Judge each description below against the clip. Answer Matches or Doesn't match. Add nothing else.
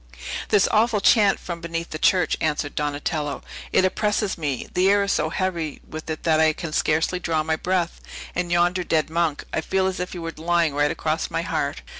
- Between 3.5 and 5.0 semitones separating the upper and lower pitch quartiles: Doesn't match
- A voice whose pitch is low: Doesn't match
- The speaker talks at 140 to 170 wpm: Doesn't match